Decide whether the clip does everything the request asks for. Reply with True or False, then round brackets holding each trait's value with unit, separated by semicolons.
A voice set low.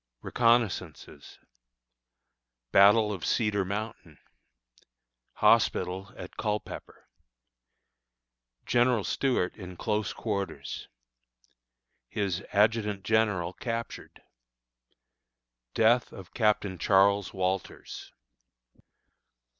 True (105 Hz)